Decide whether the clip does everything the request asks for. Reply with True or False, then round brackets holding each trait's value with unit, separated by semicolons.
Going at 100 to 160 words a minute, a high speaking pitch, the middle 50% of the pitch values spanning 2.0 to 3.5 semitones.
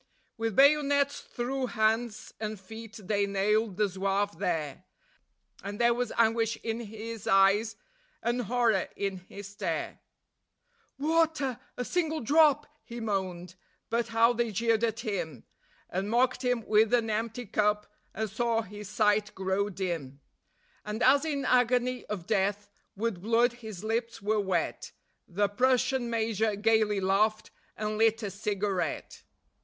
True (140 wpm; 220 Hz; 2.8 semitones)